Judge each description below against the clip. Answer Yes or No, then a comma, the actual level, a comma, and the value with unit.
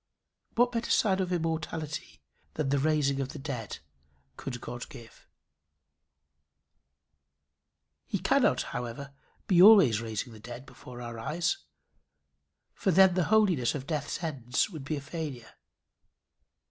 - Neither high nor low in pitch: Yes, medium, 145 Hz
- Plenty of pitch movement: Yes, wide, 5.9 semitones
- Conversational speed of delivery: No, slow, 130 wpm